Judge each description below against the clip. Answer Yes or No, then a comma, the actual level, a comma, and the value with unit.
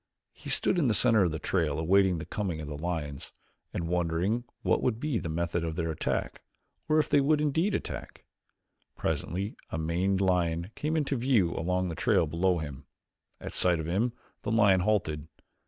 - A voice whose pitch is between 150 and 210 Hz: No, very low, 90 Hz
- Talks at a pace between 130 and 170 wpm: No, average, 190 wpm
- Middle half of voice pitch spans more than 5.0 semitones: Yes, wide, 5.4 semitones